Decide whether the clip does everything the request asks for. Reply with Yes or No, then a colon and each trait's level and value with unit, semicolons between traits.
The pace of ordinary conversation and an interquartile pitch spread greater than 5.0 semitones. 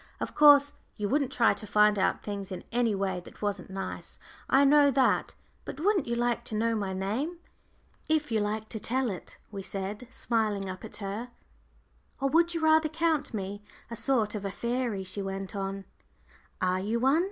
Yes: average, 190 wpm; wide, 5.4 semitones